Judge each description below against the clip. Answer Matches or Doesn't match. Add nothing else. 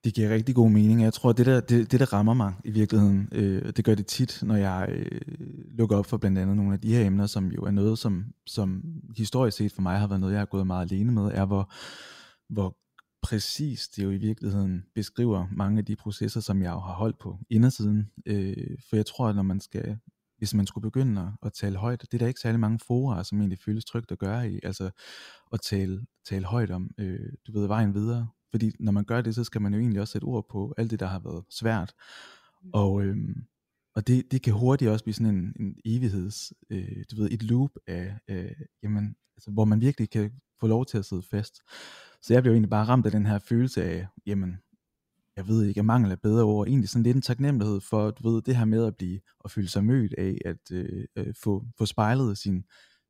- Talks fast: Matches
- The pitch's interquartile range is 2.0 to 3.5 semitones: Matches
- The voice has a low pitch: Matches